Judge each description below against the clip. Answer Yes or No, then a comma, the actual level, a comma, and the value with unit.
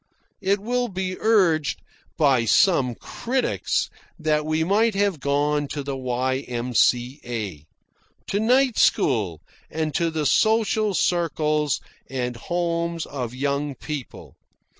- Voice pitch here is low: No, medium, 150 Hz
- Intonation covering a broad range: Yes, wide, 6.4 semitones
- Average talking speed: No, slow, 115 wpm